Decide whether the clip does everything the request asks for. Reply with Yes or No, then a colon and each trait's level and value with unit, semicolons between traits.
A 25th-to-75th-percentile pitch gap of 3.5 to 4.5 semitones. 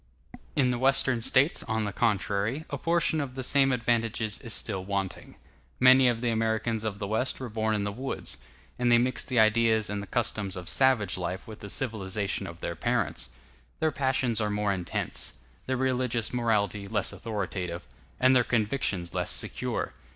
Yes: average, 3.8 semitones